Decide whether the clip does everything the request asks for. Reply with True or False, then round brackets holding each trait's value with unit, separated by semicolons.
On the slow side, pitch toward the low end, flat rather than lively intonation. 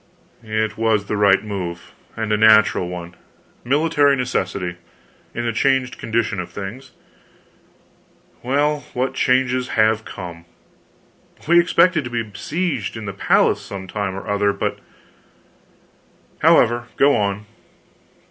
False (125 wpm; 110 Hz; 4.4 semitones)